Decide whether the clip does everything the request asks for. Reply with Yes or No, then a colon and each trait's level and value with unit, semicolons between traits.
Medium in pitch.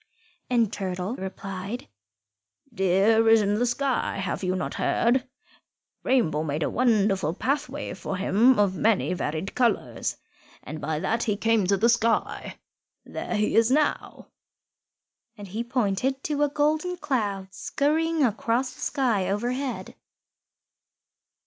No: high, 225 Hz